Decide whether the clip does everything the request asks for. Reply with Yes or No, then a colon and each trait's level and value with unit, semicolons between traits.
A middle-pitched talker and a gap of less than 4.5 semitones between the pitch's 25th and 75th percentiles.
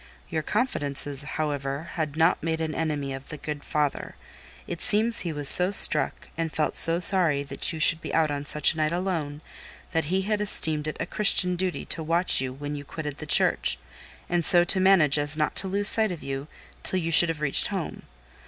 Yes: medium, 160 Hz; average, 3.5 semitones